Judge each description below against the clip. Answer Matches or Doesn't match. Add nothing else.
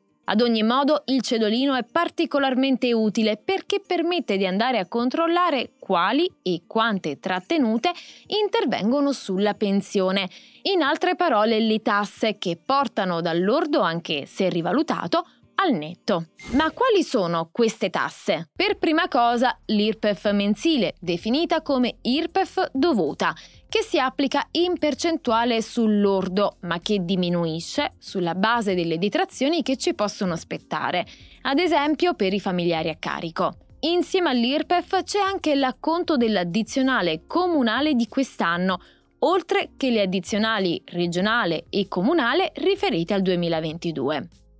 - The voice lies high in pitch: Matches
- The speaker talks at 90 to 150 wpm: Matches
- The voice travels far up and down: Matches